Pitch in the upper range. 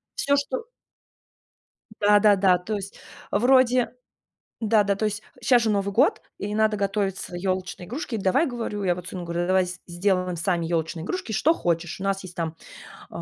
Yes: high, 200 Hz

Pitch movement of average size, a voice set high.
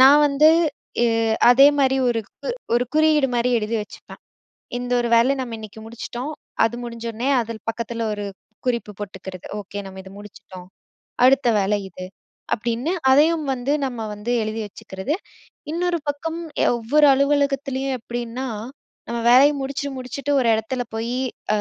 Yes: average, 3.7 semitones; high, 245 Hz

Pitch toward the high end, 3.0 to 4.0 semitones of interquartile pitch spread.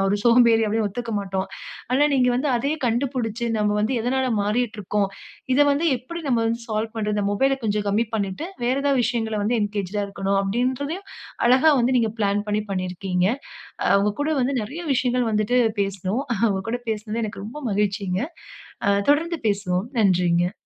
Yes: high, 220 Hz; average, 3.7 semitones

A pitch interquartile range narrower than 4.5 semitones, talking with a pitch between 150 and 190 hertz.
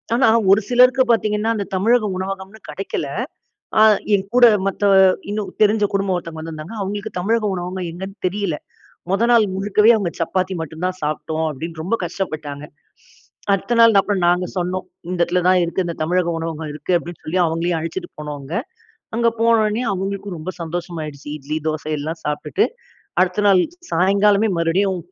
Yes: average, 3.9 semitones; medium, 185 Hz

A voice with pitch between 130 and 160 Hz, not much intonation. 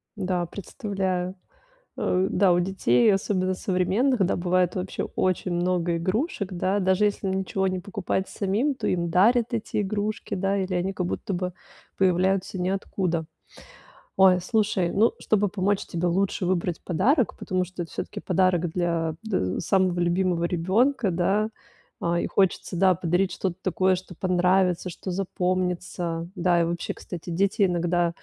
No: medium, 185 Hz; narrow, 1.8 semitones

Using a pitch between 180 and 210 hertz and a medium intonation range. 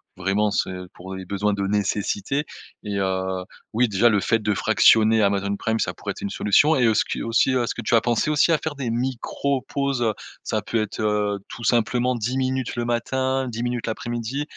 No: low, 115 Hz; average, 3.5 semitones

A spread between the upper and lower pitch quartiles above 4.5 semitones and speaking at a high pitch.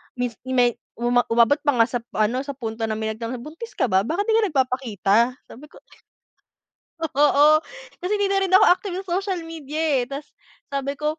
Yes: wide, 5.4 semitones; very high, 275 Hz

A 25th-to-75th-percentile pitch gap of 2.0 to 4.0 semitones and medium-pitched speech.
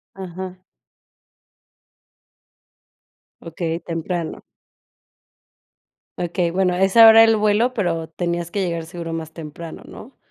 Yes: narrow, 2.6 semitones; medium, 175 Hz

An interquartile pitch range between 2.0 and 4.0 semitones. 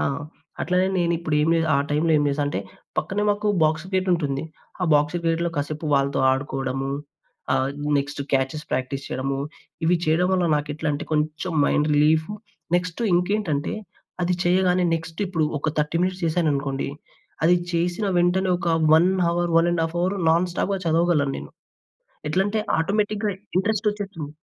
Yes: average, 3.6 semitones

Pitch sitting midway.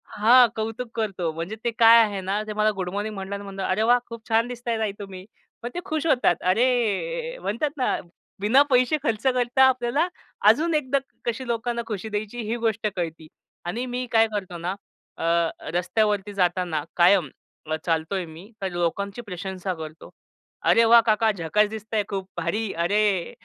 No: high, 215 Hz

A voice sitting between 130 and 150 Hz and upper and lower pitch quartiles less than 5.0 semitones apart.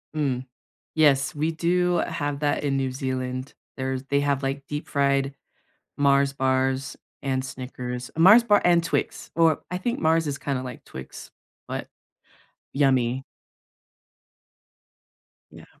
Yes: medium, 140 Hz; average, 2.8 semitones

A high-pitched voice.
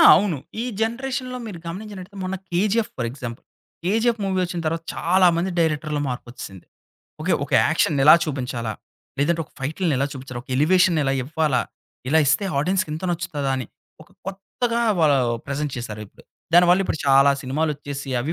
No: medium, 160 Hz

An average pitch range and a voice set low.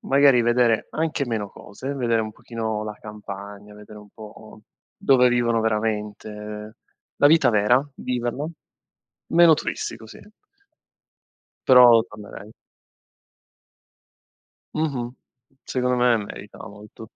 Yes: average, 3.0 semitones; low, 115 Hz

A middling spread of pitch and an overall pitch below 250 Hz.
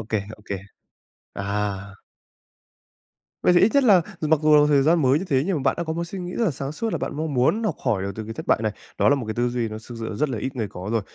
No: wide, 6.9 semitones; medium, 140 Hz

